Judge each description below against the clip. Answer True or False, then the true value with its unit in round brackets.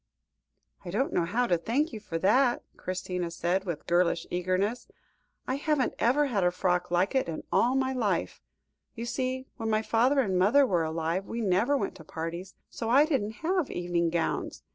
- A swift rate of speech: False (185 wpm)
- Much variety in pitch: True (6.5 semitones)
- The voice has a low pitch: False (200 Hz)